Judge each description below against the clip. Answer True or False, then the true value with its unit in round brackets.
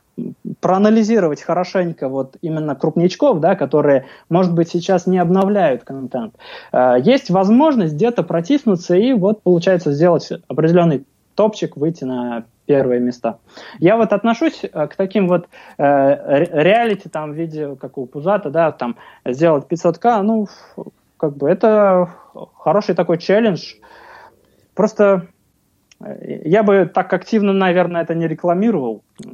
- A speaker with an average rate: True (125 wpm)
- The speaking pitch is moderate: True (175 Hz)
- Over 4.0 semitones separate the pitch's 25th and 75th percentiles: True (5.2 semitones)